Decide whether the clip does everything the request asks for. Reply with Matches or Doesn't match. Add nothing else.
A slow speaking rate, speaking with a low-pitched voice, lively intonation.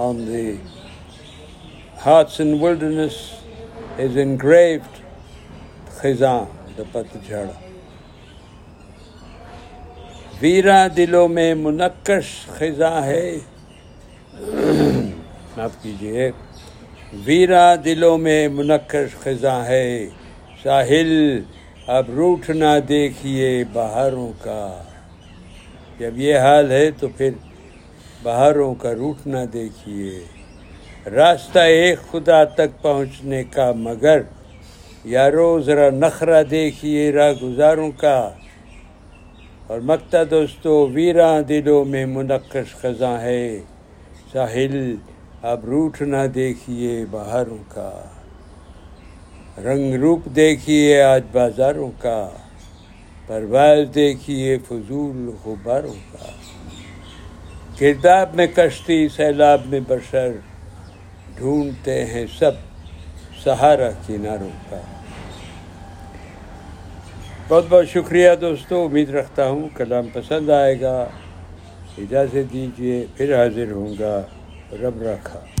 Matches